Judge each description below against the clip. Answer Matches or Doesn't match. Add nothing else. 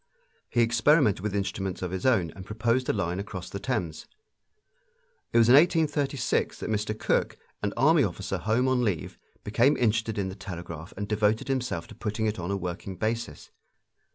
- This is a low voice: Matches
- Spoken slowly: Doesn't match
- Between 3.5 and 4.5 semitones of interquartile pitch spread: Matches